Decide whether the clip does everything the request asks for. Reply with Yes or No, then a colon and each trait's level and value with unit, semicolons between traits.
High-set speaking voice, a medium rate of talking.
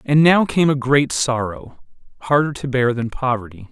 No: low, 130 Hz; average, 180 wpm